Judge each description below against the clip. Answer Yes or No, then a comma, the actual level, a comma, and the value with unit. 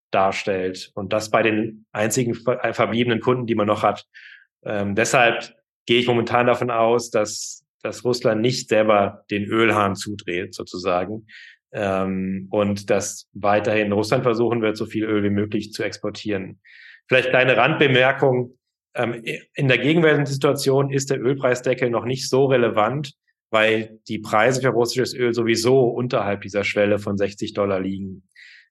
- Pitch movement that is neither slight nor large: Yes, average, 3.4 semitones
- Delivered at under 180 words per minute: Yes, average, 150 wpm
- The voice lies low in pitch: Yes, low, 110 Hz